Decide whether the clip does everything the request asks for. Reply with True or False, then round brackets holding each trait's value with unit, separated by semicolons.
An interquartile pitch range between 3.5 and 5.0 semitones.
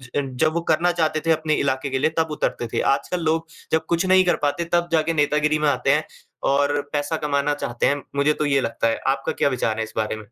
False (2.8 semitones)